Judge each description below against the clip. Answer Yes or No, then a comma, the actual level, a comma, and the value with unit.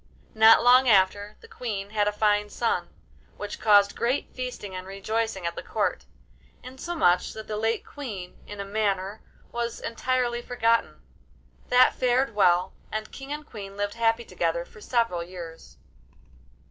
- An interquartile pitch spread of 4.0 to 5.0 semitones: No, average, 3.3 semitones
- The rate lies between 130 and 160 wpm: Yes, average, 150 wpm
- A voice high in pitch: Yes, high, 215 Hz